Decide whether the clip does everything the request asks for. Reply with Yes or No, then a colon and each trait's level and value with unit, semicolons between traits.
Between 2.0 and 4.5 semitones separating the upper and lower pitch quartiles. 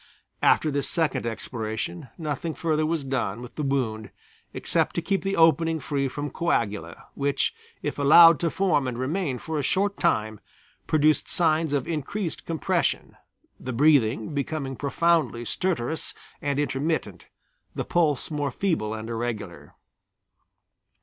No: average, 5.1 semitones